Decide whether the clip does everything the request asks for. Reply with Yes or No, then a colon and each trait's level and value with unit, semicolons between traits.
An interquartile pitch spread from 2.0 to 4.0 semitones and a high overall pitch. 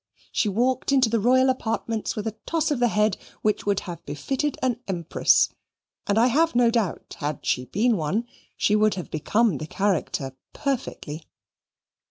No: average, 5.2 semitones; high, 220 Hz